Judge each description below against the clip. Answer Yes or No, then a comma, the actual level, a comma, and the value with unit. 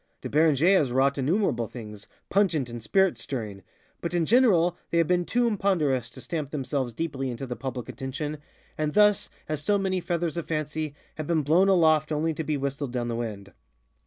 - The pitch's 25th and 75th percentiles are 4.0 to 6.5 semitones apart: Yes, average, 4.7 semitones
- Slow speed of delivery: No, average, 190 wpm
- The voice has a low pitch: No, medium, 155 Hz